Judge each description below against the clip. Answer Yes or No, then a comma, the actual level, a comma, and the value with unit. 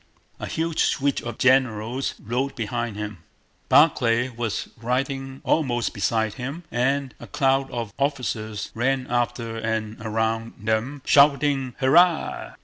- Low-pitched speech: Yes, low, 125 Hz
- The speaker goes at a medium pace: No, slow, 125 wpm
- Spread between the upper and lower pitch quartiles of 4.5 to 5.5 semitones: No, average, 3.3 semitones